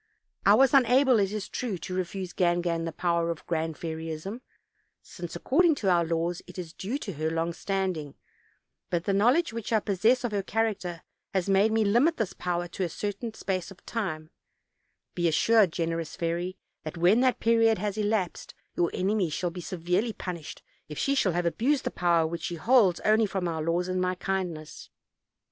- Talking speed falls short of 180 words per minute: No, average, 195 wpm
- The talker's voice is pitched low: No, medium, 185 Hz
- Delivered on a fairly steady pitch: No, average, 4.3 semitones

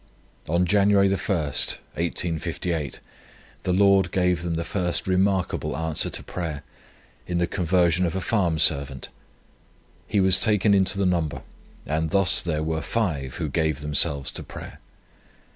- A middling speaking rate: Yes, average, 145 wpm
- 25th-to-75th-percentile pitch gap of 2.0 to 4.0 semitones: Yes, average, 3.2 semitones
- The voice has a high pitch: No, very low, 85 Hz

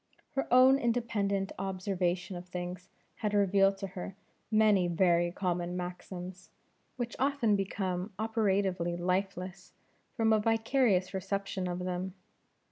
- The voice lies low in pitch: No, high, 195 Hz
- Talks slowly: Yes, slow, 120 wpm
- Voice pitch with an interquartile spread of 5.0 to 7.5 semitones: No, average, 3.0 semitones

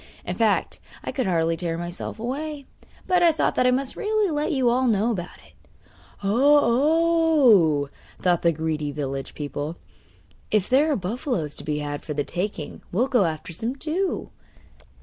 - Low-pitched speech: No, high, 220 Hz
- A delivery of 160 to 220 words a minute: Yes, average, 170 wpm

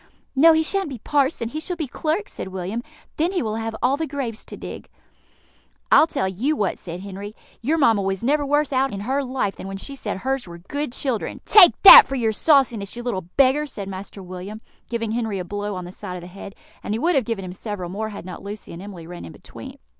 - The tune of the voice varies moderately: No, wide, 6.3 semitones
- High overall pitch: Yes, high, 225 Hz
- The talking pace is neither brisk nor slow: No, fast, 240 wpm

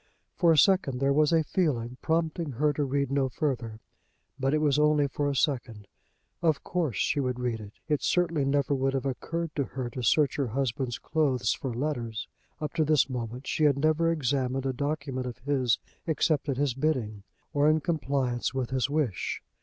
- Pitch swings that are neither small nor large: Yes, average, 3.2 semitones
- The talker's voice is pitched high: No, medium, 140 Hz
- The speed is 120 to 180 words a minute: No, average, 195 wpm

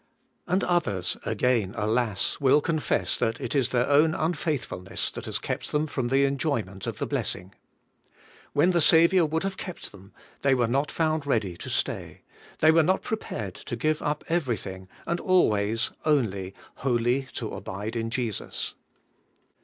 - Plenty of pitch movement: Yes, wide, 6.4 semitones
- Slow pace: No, average, 160 wpm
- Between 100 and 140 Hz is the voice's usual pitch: Yes, low, 135 Hz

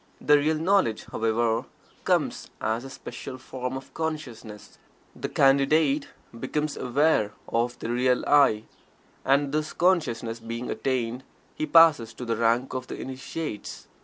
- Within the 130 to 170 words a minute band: Yes, slow, 135 wpm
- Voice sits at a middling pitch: No, low, 130 Hz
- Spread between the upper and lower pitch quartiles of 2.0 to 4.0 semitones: No, average, 4.4 semitones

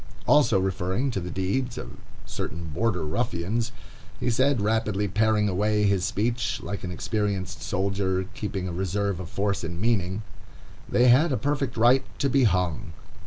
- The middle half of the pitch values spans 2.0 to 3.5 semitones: No, average, 4.1 semitones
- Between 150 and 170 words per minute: Yes, average, 160 wpm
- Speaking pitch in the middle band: No, low, 100 Hz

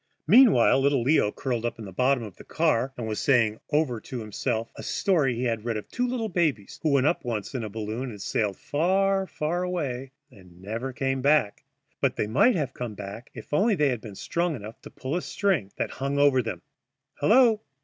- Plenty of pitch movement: Yes, wide, 6.0 semitones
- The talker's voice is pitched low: Yes, low, 130 Hz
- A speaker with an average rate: No, fast, 210 wpm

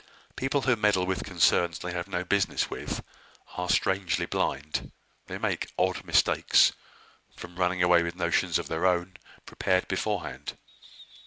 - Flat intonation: Yes, narrow, 1.5 semitones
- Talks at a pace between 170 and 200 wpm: No, average, 145 wpm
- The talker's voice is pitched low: Yes, very low, 90 Hz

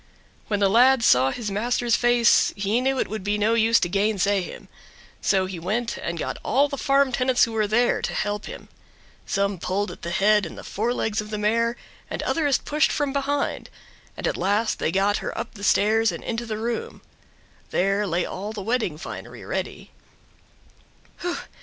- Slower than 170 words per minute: No, average, 190 wpm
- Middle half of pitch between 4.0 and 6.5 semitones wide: No, average, 3.3 semitones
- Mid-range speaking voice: No, high, 215 Hz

